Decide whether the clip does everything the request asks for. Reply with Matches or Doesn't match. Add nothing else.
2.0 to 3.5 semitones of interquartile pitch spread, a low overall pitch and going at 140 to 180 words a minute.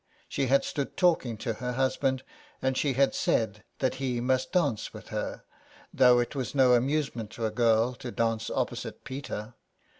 Matches